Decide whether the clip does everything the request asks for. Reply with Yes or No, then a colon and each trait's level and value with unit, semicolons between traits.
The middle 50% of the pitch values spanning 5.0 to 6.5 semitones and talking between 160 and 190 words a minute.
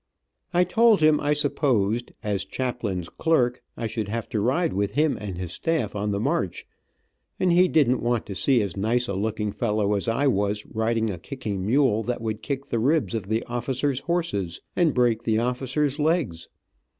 Yes: average, 5.3 semitones; average, 185 wpm